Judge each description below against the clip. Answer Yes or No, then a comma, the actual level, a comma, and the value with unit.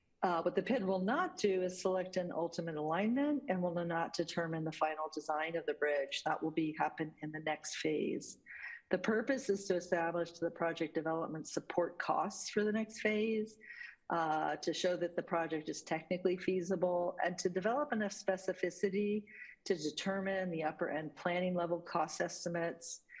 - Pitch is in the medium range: Yes, medium, 175 Hz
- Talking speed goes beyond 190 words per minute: No, average, 175 wpm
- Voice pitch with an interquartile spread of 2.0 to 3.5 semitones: Yes, average, 3.2 semitones